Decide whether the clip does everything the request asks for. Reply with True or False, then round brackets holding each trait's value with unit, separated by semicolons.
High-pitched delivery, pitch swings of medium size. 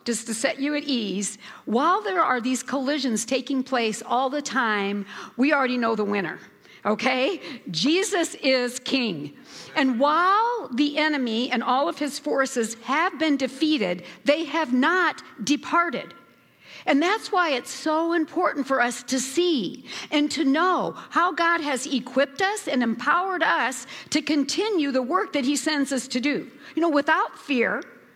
True (275 Hz; 4.1 semitones)